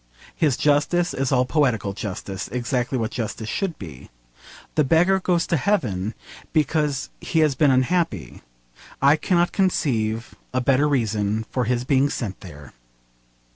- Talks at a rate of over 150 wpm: No, average, 140 wpm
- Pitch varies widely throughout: Yes, wide, 5.9 semitones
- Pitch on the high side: No, low, 130 Hz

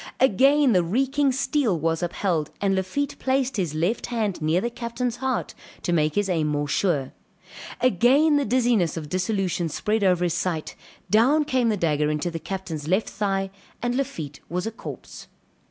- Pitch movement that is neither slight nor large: No, wide, 6.6 semitones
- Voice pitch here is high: Yes, high, 195 Hz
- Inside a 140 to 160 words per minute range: No, average, 170 wpm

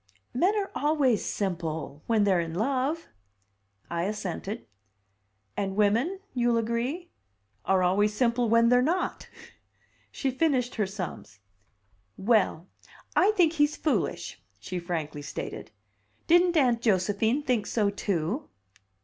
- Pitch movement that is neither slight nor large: No, wide, 6.2 semitones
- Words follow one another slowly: Yes, slow, 120 wpm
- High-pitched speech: Yes, high, 230 Hz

